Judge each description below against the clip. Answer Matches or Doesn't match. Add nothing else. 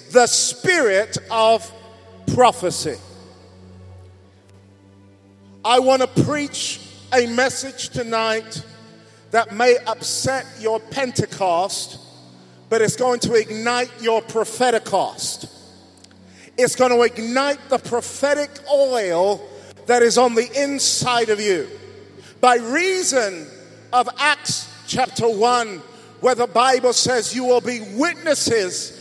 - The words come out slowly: Matches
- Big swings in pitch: Matches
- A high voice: Matches